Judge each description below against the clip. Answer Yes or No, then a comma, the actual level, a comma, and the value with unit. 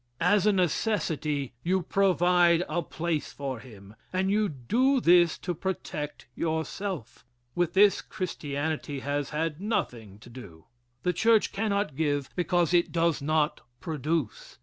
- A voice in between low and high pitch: Yes, medium, 165 Hz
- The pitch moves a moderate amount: Yes, average, 4.5 semitones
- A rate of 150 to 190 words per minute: No, slow, 135 wpm